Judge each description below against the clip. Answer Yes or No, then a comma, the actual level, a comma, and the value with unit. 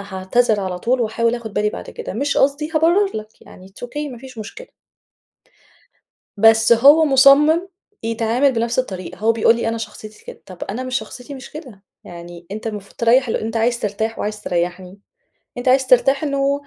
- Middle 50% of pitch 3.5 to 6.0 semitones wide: Yes, average, 4.2 semitones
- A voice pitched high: Yes, high, 230 Hz